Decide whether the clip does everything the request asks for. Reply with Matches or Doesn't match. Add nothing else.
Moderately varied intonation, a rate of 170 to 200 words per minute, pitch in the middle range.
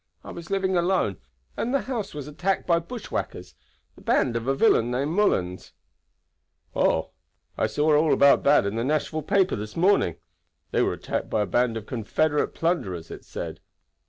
Doesn't match